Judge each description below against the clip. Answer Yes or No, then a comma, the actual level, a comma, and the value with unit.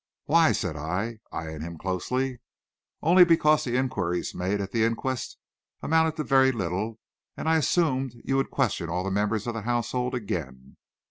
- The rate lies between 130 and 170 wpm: Yes, average, 165 wpm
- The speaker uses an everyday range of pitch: No, wide, 6.5 semitones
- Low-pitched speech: Yes, low, 115 Hz